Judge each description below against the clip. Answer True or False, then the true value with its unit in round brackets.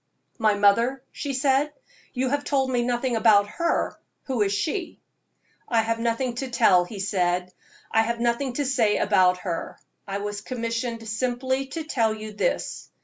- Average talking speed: True (165 wpm)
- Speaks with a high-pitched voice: True (235 Hz)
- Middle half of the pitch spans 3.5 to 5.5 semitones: True (4.0 semitones)